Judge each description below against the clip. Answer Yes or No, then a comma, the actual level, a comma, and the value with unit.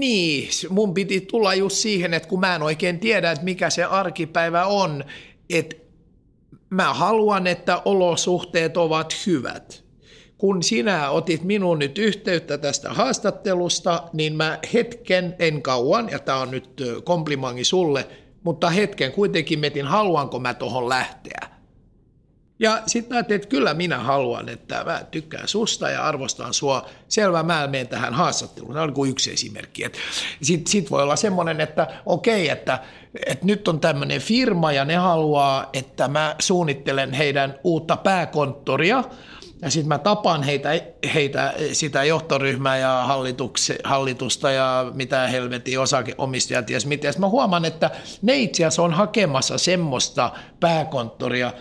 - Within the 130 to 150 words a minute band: Yes, average, 140 wpm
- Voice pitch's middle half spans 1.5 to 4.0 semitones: No, average, 5.2 semitones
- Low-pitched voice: No, medium, 165 Hz